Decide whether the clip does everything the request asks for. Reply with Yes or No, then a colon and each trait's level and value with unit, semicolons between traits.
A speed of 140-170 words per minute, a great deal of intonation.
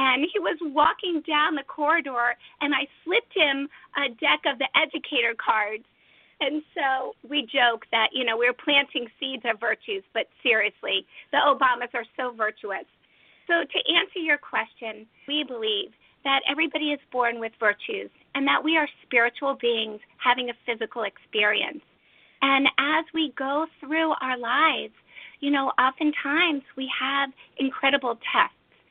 No: average, 150 wpm; average, 4.1 semitones